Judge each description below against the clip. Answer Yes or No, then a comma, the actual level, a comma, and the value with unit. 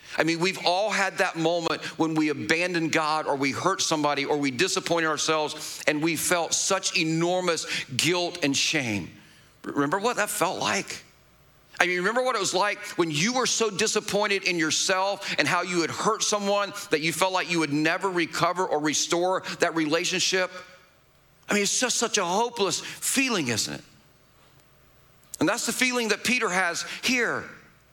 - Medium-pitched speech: Yes, medium, 180 Hz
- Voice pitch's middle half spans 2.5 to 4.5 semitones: Yes, average, 4.0 semitones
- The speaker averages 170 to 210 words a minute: Yes, average, 175 wpm